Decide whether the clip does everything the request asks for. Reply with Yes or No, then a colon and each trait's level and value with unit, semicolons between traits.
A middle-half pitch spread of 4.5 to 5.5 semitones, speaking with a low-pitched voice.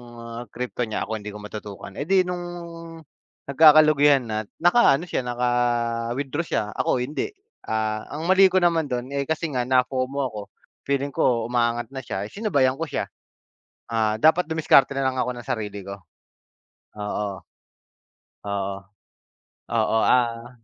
Yes: average, 4.9 semitones; low, 125 Hz